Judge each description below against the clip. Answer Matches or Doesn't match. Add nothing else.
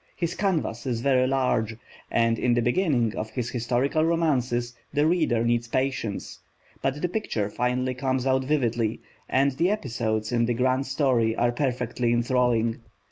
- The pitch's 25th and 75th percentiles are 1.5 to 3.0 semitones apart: Matches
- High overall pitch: Doesn't match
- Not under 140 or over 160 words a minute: Matches